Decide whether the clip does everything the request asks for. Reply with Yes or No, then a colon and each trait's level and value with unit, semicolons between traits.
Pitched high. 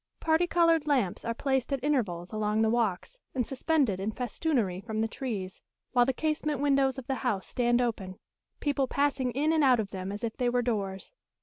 Yes: high, 245 Hz